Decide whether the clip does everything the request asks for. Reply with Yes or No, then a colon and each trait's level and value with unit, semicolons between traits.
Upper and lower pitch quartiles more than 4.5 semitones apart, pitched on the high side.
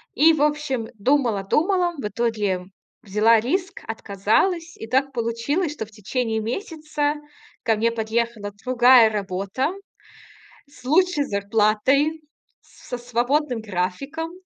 Yes: wide, 5.5 semitones; high, 240 Hz